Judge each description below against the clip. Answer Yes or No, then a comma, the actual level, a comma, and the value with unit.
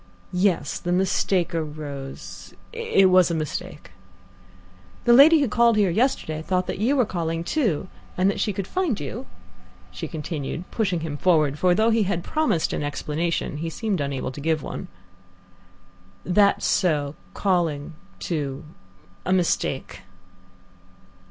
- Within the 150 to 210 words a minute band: No, average, 140 wpm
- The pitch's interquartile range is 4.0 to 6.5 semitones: Yes, average, 5.0 semitones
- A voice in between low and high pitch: Yes, medium, 175 Hz